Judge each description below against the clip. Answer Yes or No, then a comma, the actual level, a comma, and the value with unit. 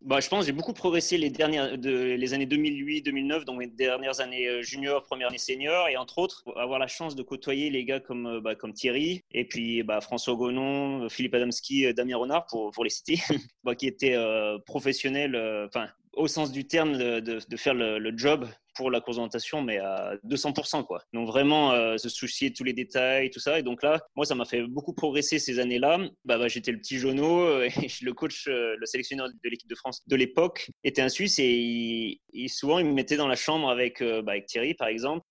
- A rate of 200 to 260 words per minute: Yes, average, 215 wpm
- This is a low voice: Yes, low, 130 Hz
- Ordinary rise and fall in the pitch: Yes, average, 3.5 semitones